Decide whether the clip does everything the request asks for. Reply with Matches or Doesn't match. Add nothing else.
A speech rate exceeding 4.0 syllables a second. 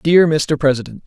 Matches